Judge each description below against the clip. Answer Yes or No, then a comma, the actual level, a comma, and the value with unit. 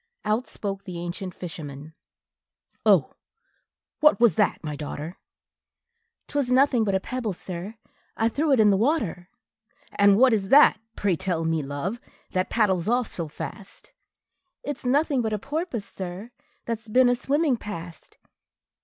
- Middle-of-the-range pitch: No, high, 210 Hz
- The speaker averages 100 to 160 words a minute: Yes, average, 155 wpm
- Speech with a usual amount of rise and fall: No, wide, 5.8 semitones